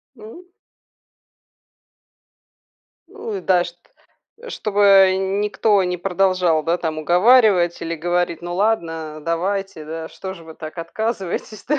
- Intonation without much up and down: No, average, 3.7 semitones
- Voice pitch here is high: No, medium, 180 Hz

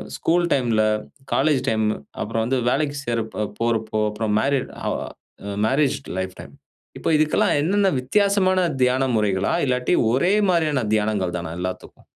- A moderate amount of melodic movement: No, wide, 5.9 semitones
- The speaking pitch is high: No, low, 125 Hz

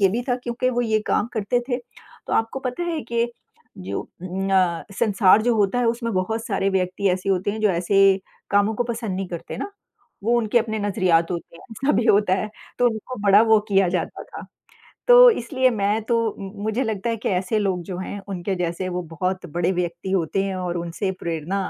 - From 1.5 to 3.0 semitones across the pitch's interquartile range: No, average, 3.8 semitones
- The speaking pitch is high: Yes, high, 200 Hz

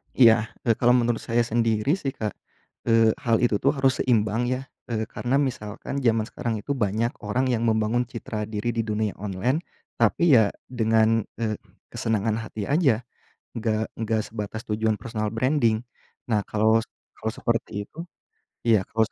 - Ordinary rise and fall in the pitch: No, narrow, 2.0 semitones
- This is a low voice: Yes, low, 115 Hz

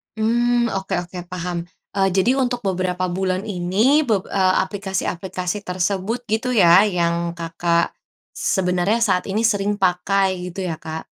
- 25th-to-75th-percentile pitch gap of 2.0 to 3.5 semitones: Yes, average, 2.7 semitones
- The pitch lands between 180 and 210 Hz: Yes, high, 190 Hz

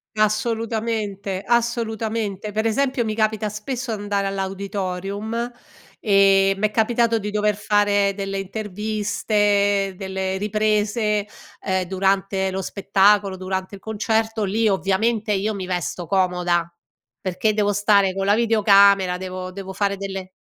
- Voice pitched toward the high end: Yes, high, 205 Hz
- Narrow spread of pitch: Yes, narrow, 2.0 semitones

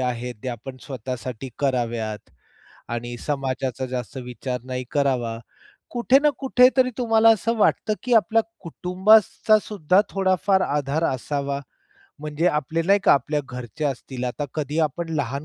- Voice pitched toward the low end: No, medium, 145 Hz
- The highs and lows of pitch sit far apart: Yes, wide, 7.0 semitones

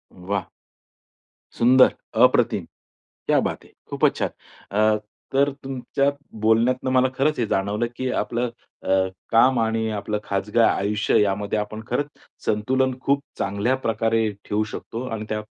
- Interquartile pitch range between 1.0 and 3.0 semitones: No, average, 3.5 semitones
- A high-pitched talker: No, low, 115 Hz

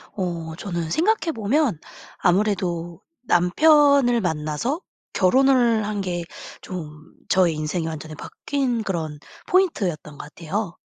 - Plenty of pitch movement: Yes, wide, 6.9 semitones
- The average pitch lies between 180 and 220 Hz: Yes, medium, 185 Hz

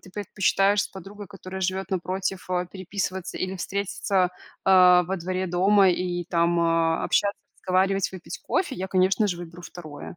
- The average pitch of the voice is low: No, medium, 185 Hz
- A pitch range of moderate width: No, narrow, 1.6 semitones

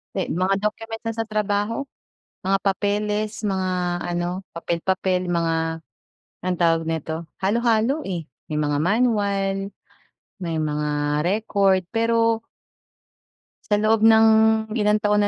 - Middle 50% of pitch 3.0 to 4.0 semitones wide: Yes, average, 3.5 semitones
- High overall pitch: Yes, high, 200 Hz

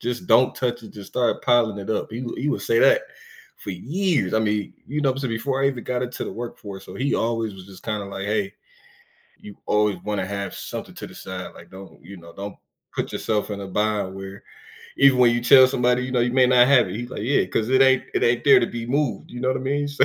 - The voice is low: Yes, low, 120 Hz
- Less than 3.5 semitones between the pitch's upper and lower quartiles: No, average, 4.0 semitones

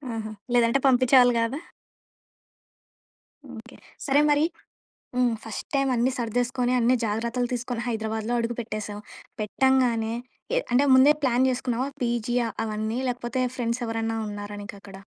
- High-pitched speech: Yes, high, 240 Hz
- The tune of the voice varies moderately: No, narrow, 2.2 semitones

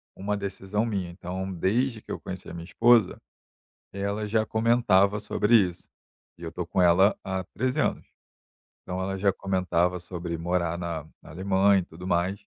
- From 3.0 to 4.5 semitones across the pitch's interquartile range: No, narrow, 2.6 semitones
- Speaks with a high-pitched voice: No, very low, 95 Hz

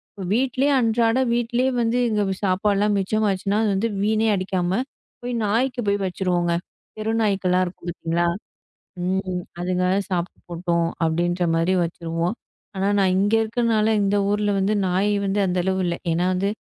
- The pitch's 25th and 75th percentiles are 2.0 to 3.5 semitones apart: Yes, average, 3.2 semitones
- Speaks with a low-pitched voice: No, high, 195 Hz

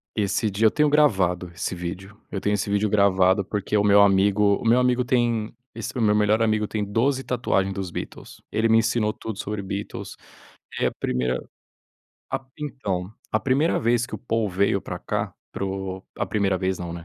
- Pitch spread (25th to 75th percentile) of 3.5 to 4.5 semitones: No, average, 2.9 semitones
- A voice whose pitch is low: Yes, low, 105 Hz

